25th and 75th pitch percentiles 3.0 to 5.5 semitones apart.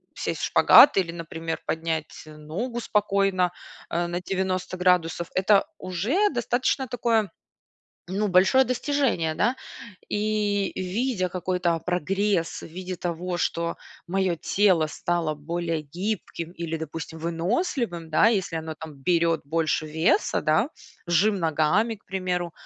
Yes: average, 3.6 semitones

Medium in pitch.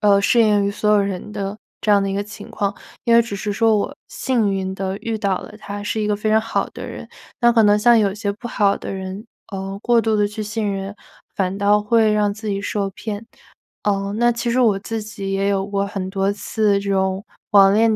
No: high, 205 Hz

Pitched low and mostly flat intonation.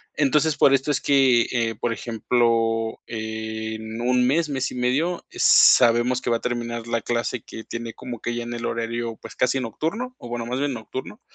Yes: low, 120 Hz; narrow, 2.2 semitones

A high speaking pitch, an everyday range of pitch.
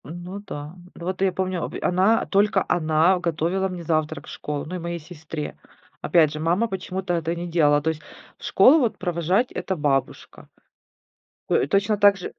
No: medium, 175 Hz; average, 3.3 semitones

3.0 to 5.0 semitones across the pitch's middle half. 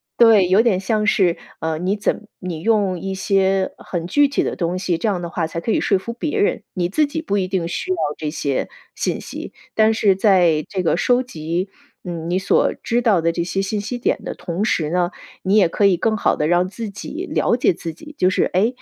Yes: average, 3.8 semitones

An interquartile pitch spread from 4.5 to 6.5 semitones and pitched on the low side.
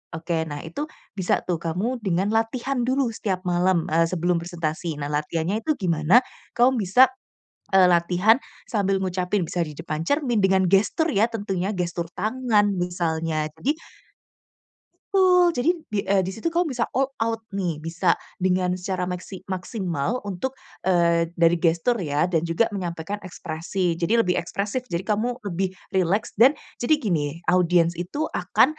No: average, 4.9 semitones; medium, 185 Hz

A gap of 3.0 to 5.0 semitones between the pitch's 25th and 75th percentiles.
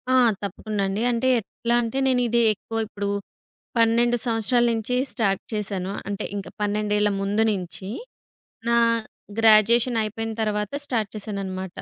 No: narrow, 2.4 semitones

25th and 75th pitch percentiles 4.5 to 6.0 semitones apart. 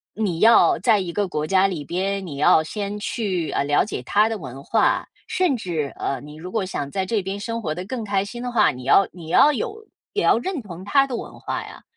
Yes: wide, 5.5 semitones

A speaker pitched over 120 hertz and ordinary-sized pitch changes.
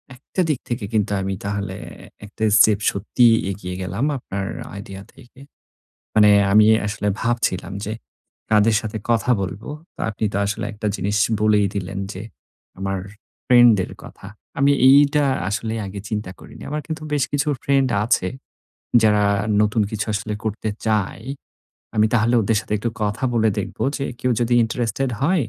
No: low, 110 Hz; average, 3.2 semitones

